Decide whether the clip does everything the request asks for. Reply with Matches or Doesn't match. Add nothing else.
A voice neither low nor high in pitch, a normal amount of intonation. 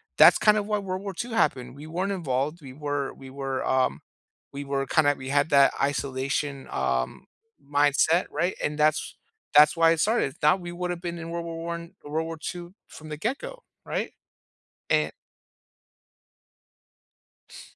Matches